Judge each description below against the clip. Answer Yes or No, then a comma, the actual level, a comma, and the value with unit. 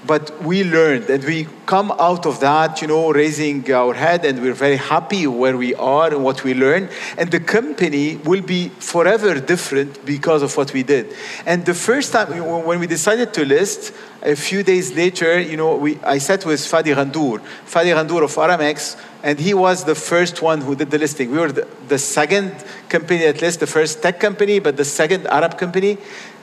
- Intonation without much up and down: No, average, 3.7 semitones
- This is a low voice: No, medium, 160 Hz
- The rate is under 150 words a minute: No, fast, 205 wpm